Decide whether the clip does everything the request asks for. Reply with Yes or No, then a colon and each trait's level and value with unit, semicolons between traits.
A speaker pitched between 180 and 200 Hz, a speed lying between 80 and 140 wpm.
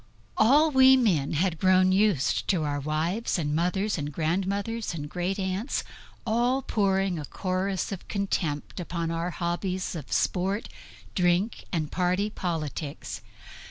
Yes: medium, 185 Hz; slow, 135 wpm